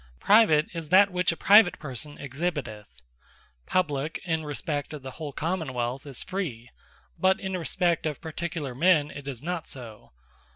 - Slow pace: No, average, 160 wpm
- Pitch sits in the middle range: Yes, medium, 155 Hz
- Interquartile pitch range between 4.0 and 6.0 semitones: Yes, average, 4.6 semitones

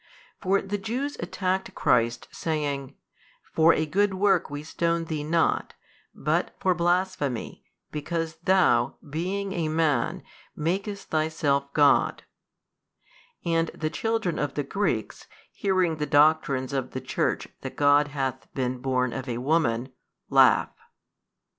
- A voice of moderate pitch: Yes, medium, 155 Hz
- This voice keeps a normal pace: No, slow, 130 wpm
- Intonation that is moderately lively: Yes, average, 4.6 semitones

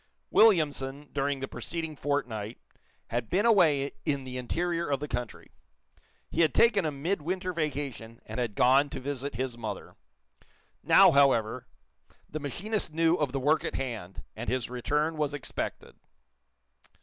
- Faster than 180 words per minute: No, average, 150 wpm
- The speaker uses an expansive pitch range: No, average, 4.1 semitones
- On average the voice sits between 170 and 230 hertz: No, medium, 140 Hz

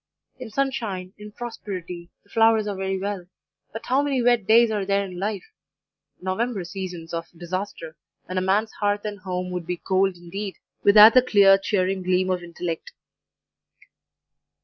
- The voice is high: Yes, high, 195 Hz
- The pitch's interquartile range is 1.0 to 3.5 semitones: Yes, average, 2.8 semitones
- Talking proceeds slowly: No, average, 160 wpm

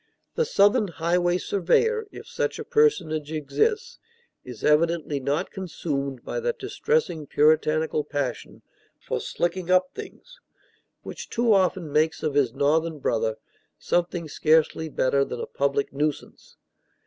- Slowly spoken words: Yes, slow, 130 wpm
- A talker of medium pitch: Yes, medium, 160 Hz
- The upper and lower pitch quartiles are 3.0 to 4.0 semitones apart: No, average, 4.5 semitones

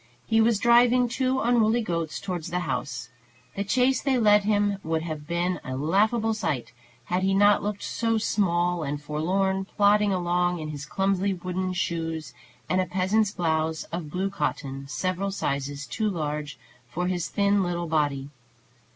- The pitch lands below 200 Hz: Yes, medium, 185 Hz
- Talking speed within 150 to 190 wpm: Yes, average, 160 wpm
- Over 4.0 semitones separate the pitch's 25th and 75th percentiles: Yes, average, 4.5 semitones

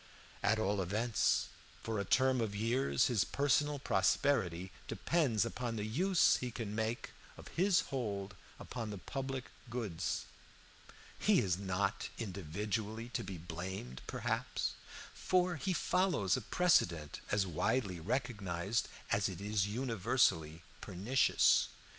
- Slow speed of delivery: Yes, slow, 125 wpm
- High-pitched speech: No, low, 110 Hz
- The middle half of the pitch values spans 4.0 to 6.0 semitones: Yes, average, 5.1 semitones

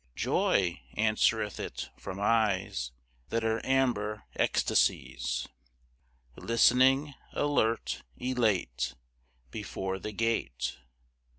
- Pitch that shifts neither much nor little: Yes, average, 3.6 semitones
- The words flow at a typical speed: No, slow, 80 wpm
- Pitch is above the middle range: No, low, 110 Hz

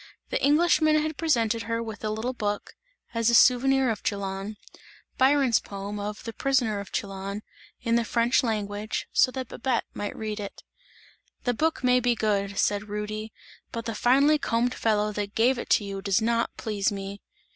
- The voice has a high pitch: Yes, high, 225 Hz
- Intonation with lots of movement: No, average, 3.3 semitones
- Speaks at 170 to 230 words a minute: Yes, average, 180 wpm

